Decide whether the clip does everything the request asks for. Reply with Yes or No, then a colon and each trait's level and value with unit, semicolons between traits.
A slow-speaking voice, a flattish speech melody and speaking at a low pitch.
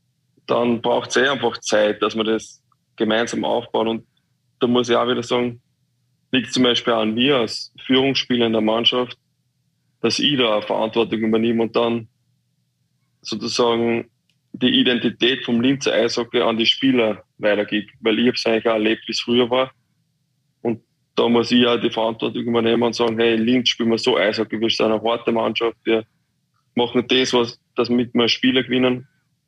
No: average, 185 wpm; narrow, 2.0 semitones; low, 120 Hz